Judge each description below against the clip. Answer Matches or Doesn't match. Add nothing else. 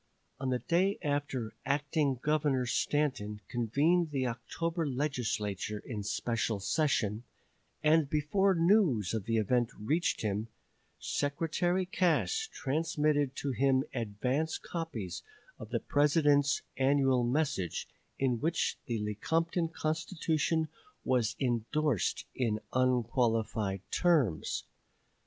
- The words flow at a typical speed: Doesn't match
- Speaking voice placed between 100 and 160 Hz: Matches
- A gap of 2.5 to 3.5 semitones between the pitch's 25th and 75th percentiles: Doesn't match